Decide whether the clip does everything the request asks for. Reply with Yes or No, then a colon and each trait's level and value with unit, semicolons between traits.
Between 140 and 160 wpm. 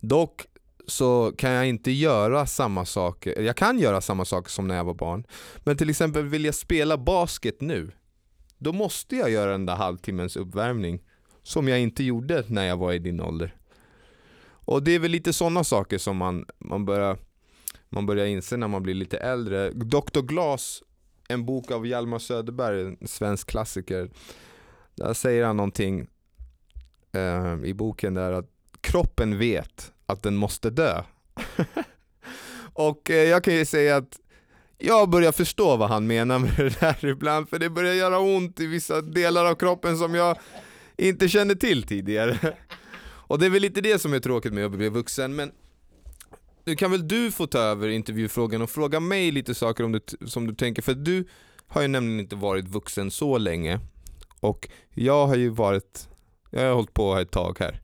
No: average, 180 wpm